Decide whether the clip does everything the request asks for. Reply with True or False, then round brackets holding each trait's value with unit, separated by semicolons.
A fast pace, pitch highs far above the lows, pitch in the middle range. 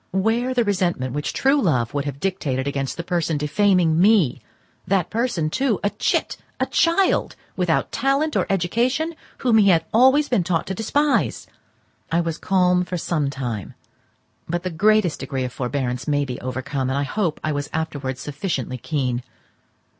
False (165 wpm; 7.0 semitones; 170 Hz)